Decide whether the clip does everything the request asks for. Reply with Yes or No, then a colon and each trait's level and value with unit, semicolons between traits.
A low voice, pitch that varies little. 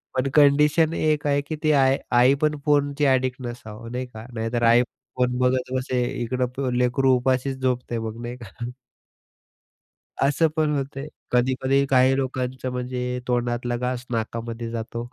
Yes: low, 125 Hz; narrow, 2.1 semitones